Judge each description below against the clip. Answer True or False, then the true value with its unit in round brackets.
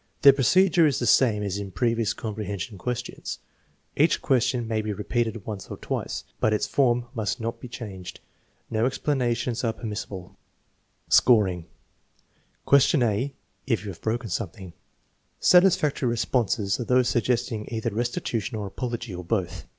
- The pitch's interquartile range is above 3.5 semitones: False (3.2 semitones)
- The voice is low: True (115 Hz)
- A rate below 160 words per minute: True (150 wpm)